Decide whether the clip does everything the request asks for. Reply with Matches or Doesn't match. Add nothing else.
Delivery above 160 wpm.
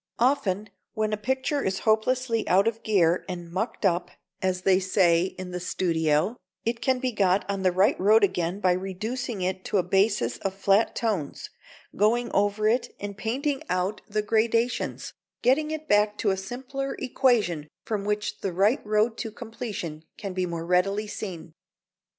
Matches